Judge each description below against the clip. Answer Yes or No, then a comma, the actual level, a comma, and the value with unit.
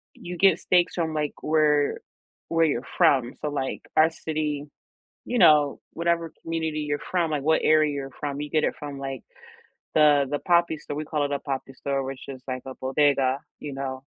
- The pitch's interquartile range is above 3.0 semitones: No, narrow, 2.5 semitones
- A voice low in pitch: No, medium, 150 Hz